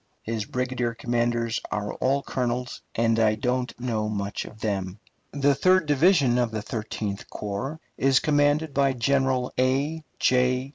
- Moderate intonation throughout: Yes, average, 3.6 semitones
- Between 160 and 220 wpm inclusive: No, average, 145 wpm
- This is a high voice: No, low, 125 Hz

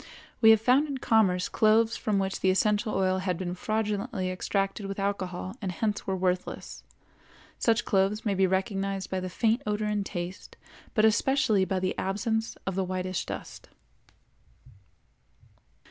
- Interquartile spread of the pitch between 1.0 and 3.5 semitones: Yes, narrow, 2.6 semitones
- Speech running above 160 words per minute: No, average, 155 wpm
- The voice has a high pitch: Yes, high, 195 Hz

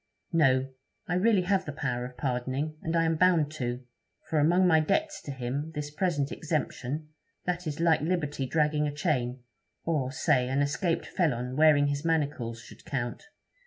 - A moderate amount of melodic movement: Yes, average, 3.7 semitones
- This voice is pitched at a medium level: Yes, medium, 150 Hz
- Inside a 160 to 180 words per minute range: Yes, average, 170 wpm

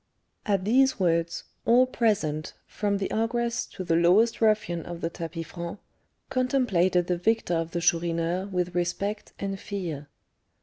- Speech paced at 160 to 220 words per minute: No, average, 145 wpm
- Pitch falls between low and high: Yes, medium, 180 Hz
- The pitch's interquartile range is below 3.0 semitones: No, average, 4.2 semitones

